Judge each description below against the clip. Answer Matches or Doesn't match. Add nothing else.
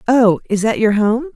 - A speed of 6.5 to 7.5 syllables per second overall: Doesn't match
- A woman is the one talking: Matches